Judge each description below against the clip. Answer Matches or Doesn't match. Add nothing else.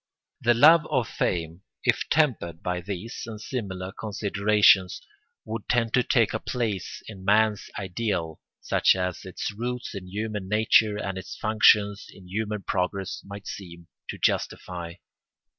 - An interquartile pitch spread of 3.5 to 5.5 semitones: Doesn't match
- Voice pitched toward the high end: Doesn't match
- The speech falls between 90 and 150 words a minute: Matches